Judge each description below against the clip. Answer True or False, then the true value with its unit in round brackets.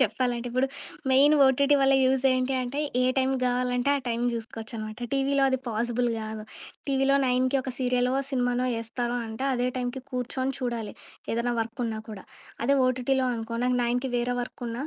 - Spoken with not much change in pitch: True (2.0 semitones)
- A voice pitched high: True (250 Hz)